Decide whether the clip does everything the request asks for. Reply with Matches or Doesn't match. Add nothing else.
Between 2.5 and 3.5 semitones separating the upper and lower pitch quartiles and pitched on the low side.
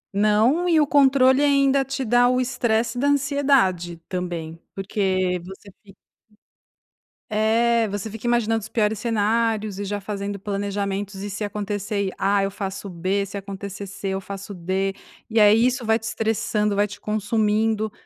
Doesn't match